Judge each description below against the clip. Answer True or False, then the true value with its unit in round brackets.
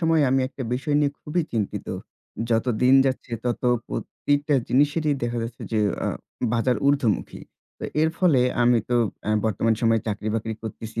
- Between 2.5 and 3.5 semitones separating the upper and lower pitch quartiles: False (4.2 semitones)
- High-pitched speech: False (125 Hz)